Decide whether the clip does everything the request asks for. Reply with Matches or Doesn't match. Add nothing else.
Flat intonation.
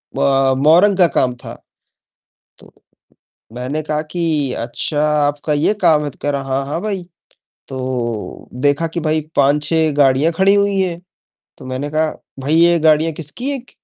Doesn't match